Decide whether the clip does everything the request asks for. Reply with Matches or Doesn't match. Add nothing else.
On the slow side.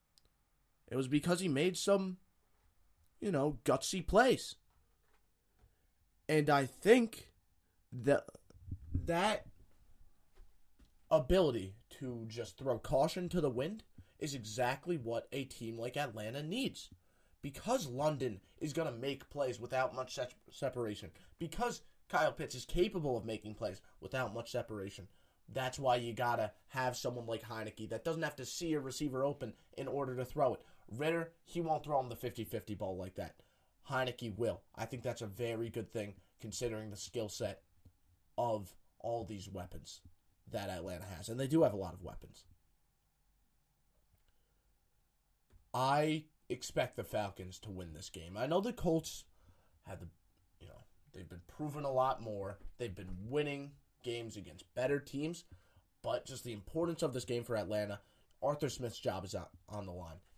Doesn't match